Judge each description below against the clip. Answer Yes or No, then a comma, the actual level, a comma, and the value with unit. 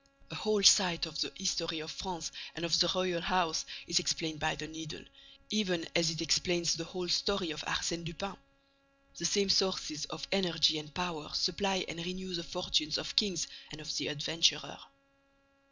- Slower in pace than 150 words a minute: No, average, 175 wpm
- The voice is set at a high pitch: No, medium, 170 Hz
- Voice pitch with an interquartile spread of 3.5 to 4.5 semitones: No, average, 2.7 semitones